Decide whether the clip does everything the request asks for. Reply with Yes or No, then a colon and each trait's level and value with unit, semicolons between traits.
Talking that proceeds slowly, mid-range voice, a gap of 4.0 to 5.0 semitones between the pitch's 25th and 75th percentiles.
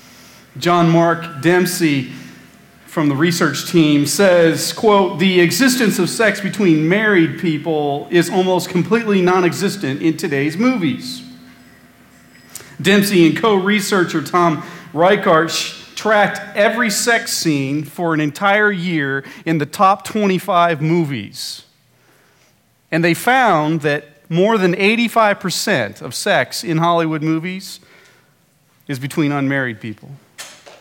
Yes: slow, 110 wpm; medium, 170 Hz; average, 4.5 semitones